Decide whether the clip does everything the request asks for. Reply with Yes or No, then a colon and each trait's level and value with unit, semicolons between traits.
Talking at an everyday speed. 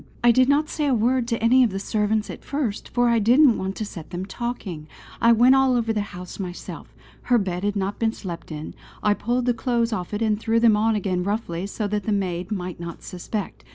No: fast, 235 wpm